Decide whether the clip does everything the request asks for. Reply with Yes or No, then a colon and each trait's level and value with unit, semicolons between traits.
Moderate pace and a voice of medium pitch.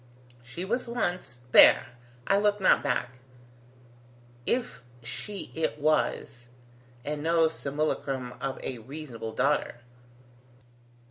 No: slow, 105 wpm; medium, 150 Hz